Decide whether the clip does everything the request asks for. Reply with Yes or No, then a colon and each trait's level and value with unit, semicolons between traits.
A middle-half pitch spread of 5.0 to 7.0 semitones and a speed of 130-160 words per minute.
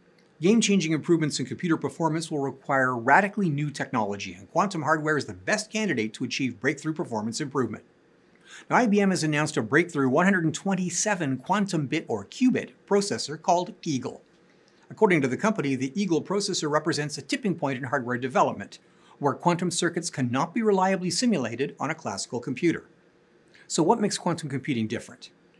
Yes: wide, 5.6 semitones; average, 155 wpm